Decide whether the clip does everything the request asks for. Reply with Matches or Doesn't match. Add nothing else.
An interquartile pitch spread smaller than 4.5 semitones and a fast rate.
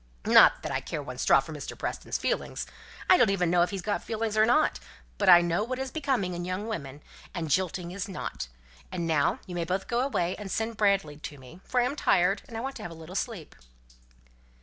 Doesn't match